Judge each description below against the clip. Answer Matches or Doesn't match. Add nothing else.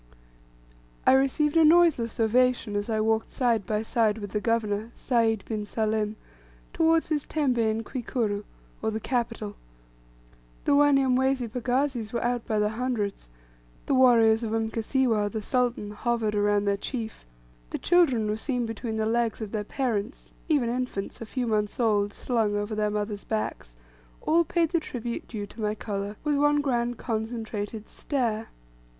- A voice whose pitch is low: Doesn't match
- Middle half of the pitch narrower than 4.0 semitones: Matches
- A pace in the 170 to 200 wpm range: Doesn't match